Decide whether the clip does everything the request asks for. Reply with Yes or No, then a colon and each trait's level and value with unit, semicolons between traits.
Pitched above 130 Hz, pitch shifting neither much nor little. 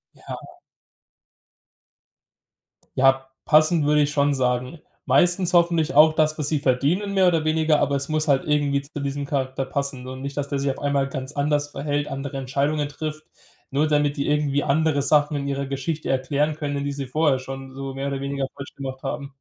No: medium, 140 Hz; narrow, 1.9 semitones